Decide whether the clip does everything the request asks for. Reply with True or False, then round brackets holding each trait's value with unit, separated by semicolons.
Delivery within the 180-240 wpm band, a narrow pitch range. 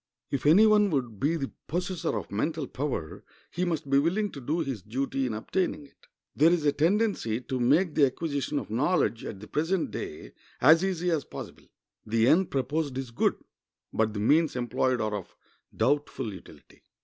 False (185 wpm; 5.4 semitones)